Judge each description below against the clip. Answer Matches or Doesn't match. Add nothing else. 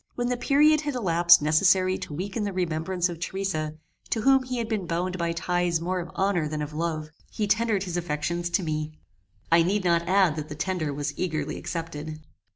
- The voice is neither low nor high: Matches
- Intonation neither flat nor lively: Matches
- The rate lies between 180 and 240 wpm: Matches